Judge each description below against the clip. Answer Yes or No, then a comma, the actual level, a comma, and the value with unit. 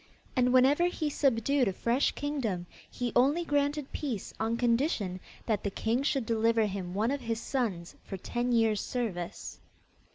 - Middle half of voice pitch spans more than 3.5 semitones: Yes, average, 4.2 semitones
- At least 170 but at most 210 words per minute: No, average, 160 wpm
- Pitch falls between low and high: No, high, 235 Hz